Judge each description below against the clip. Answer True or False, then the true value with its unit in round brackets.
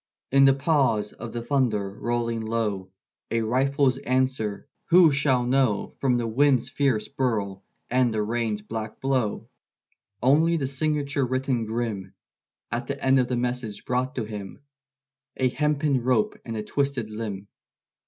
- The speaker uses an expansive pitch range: False (3.7 semitones)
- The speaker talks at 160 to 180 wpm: False (145 wpm)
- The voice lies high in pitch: False (125 Hz)